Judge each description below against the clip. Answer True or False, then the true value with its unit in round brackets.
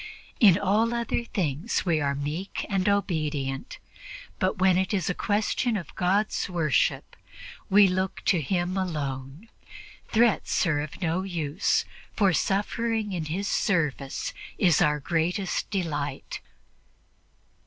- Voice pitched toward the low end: False (180 Hz)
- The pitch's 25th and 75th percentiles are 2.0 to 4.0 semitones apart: False (4.6 semitones)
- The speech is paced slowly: True (125 wpm)